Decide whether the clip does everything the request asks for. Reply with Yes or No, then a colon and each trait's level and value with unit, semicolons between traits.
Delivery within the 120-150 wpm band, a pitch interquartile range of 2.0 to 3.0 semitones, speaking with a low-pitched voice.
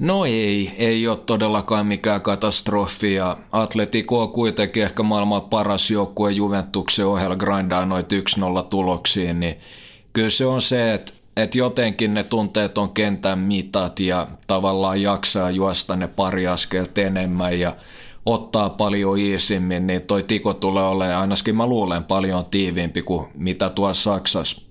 Yes: average, 145 wpm; narrow, 2.6 semitones; low, 100 Hz